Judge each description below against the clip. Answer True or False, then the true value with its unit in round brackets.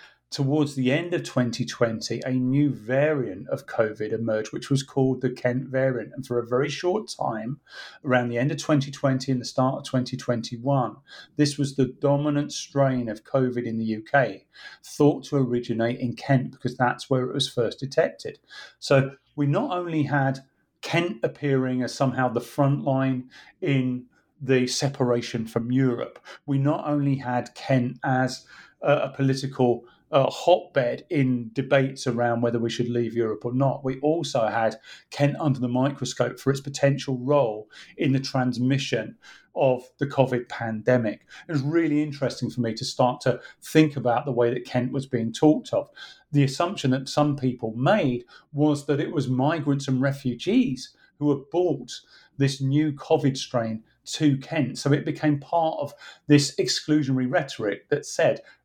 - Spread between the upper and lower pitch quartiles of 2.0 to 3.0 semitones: True (2.4 semitones)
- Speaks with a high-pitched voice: False (135 Hz)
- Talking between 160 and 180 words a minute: True (165 wpm)